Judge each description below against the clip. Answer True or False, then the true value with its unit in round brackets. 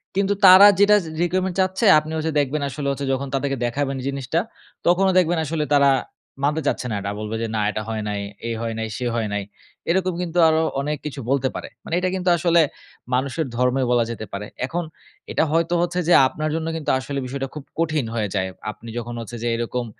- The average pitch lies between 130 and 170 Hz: True (140 Hz)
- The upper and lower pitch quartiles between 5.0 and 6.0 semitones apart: True (5.6 semitones)